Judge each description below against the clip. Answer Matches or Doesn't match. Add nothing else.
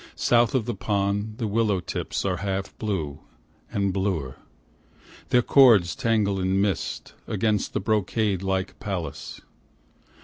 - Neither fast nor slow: Doesn't match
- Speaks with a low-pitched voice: Matches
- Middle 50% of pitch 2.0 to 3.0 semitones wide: Matches